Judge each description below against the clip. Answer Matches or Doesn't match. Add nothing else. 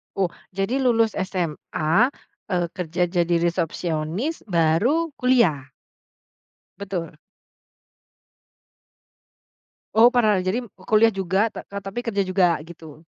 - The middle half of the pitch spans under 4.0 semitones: Doesn't match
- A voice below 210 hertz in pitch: Matches